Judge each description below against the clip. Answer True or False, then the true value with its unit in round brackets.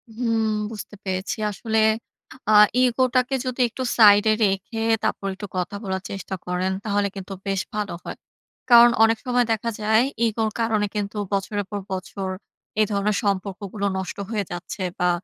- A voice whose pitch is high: True (205 Hz)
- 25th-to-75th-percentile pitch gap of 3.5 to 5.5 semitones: False (2.5 semitones)